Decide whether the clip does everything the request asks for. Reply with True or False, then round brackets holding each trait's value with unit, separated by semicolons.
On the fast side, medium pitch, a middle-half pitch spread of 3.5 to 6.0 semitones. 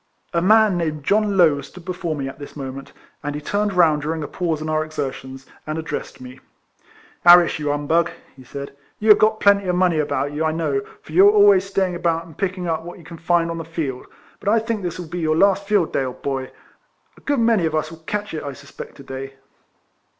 True (250 wpm; 165 Hz; 4.1 semitones)